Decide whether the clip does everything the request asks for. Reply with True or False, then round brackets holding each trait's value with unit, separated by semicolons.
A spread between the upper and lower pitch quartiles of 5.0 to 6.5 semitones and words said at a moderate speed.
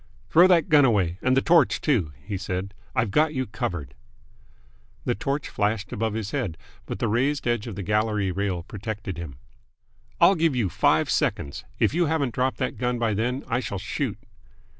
True (5.3 semitones; 185 wpm)